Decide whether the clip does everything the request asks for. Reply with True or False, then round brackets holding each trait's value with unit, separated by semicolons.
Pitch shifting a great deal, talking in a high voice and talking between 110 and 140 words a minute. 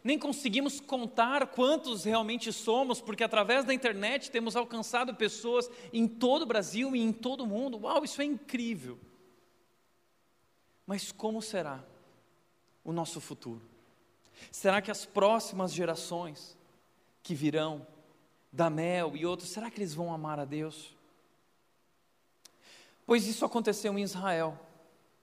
True (6.5 semitones; 210 Hz; 130 wpm)